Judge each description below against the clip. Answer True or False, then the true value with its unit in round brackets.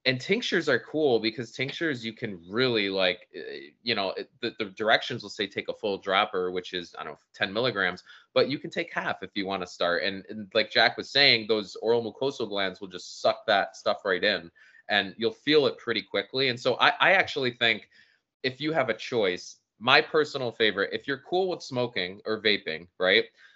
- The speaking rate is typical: False (215 wpm)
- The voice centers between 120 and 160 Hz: True (125 Hz)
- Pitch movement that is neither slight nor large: False (6.5 semitones)